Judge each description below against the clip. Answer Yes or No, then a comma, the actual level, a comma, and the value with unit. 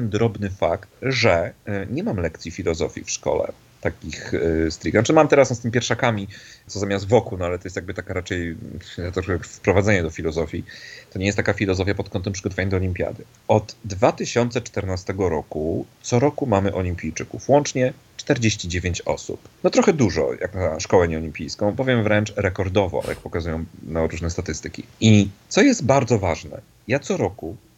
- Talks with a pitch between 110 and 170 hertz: No, low, 100 Hz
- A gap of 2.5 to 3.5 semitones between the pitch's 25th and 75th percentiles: No, average, 4.4 semitones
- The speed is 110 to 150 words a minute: No, fast, 160 wpm